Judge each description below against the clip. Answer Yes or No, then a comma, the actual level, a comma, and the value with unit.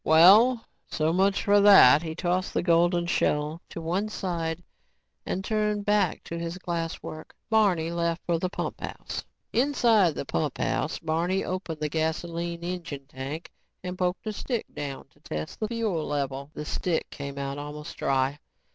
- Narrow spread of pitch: No, average, 3.6 semitones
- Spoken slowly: No, average, 160 wpm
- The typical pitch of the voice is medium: Yes, medium, 170 Hz